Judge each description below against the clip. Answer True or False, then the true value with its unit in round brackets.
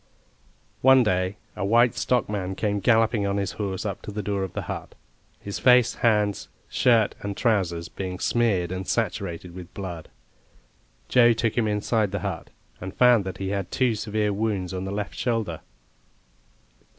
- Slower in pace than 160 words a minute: False (165 wpm)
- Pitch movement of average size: True (3.1 semitones)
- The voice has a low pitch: True (100 Hz)